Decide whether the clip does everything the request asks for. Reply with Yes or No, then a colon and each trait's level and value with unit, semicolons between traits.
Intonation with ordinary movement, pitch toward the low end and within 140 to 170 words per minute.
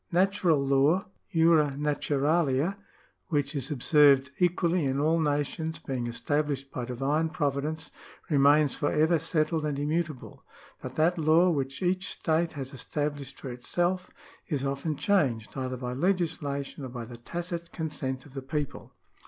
No: average, 3.3 semitones; medium, 150 Hz; average, 150 wpm